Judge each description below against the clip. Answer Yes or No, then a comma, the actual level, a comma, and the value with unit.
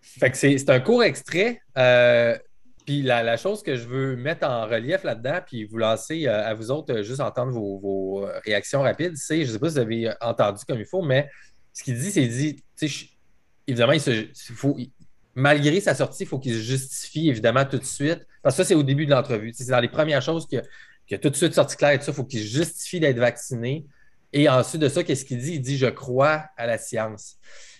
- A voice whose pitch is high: No, low, 135 Hz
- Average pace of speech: No, fast, 225 wpm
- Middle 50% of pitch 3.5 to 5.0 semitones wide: Yes, average, 4.2 semitones